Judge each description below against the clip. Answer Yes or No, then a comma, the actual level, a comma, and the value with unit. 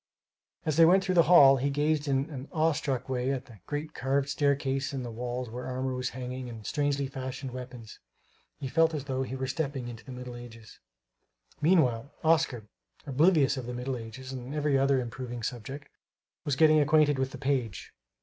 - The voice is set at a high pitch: No, low, 135 Hz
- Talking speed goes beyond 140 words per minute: Yes, average, 190 wpm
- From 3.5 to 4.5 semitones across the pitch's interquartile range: No, average, 2.7 semitones